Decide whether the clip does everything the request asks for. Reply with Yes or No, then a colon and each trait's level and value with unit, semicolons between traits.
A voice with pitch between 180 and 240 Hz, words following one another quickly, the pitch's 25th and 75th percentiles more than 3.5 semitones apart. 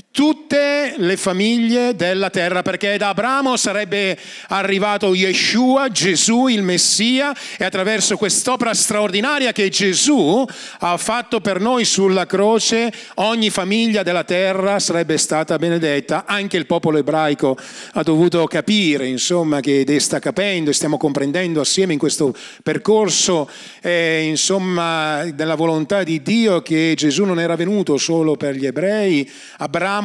No: high, 190 Hz; average, 135 wpm; average, 4.6 semitones